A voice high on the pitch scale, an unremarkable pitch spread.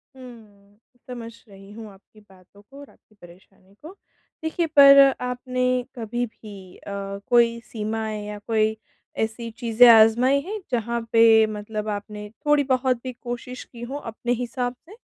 Yes: high, 230 Hz; average, 3.0 semitones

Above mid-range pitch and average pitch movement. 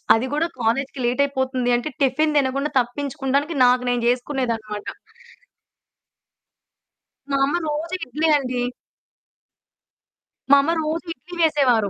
Yes: very high, 270 Hz; average, 3.2 semitones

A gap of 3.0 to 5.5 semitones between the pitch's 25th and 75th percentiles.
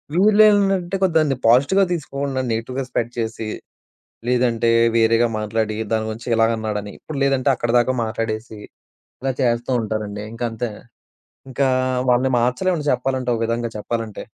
Yes: average, 3.3 semitones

